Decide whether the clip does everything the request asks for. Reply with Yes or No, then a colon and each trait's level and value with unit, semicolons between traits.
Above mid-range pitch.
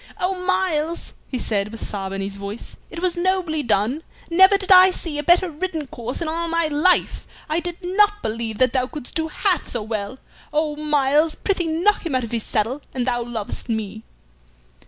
Yes: very high, 300 Hz